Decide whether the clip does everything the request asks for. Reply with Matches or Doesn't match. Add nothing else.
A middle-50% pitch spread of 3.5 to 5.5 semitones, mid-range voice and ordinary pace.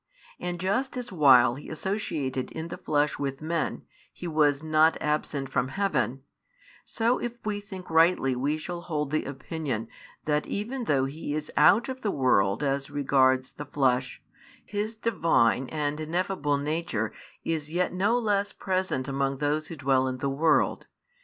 Matches